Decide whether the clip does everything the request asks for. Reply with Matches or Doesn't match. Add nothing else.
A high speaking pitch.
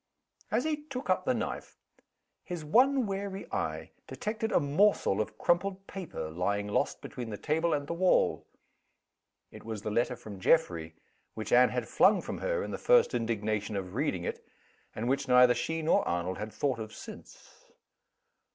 Doesn't match